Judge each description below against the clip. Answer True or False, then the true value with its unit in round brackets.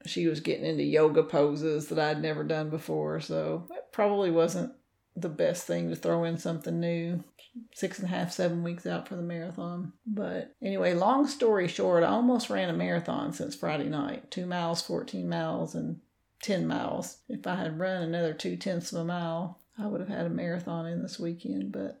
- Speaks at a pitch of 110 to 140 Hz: False (170 Hz)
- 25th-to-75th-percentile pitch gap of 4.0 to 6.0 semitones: False (2.5 semitones)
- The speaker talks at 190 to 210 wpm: True (200 wpm)